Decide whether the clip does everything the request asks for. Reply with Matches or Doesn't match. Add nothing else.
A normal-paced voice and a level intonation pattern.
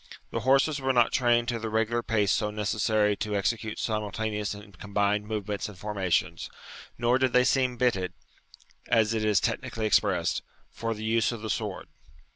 Matches